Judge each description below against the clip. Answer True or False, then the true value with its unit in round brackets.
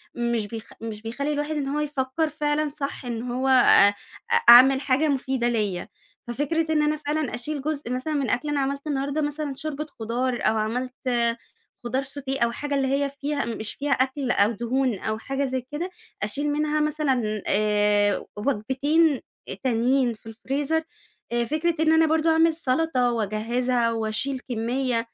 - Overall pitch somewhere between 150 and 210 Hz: False (265 Hz)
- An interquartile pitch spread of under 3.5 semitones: False (3.8 semitones)